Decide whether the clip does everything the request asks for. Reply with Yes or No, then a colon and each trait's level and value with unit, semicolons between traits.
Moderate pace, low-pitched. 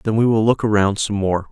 No: fast, 275 wpm; low, 105 Hz